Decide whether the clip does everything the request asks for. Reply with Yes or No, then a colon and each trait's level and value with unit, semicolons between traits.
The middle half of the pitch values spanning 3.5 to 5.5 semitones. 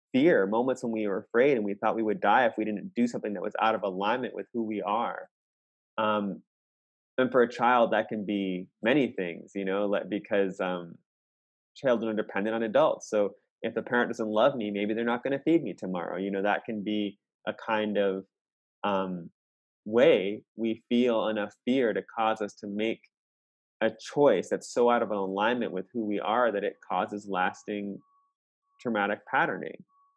No: narrow, 2.5 semitones